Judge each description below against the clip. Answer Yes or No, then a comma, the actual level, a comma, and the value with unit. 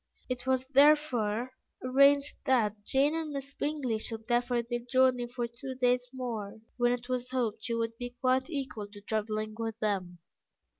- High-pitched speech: Yes, high, 245 Hz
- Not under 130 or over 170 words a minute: Yes, average, 165 wpm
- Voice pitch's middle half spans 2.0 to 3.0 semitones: Yes, average, 2.7 semitones